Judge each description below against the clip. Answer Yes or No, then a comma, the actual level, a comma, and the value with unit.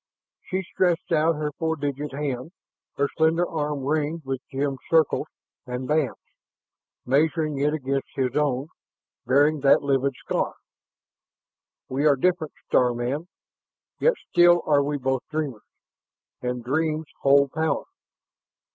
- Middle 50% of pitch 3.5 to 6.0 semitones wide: No, average, 2.8 semitones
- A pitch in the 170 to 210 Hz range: No, medium, 145 Hz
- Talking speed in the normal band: No, slow, 130 wpm